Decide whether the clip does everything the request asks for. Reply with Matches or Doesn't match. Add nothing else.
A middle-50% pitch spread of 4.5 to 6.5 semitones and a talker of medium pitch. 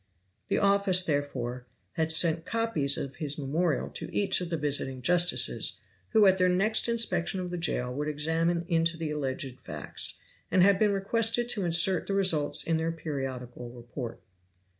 Matches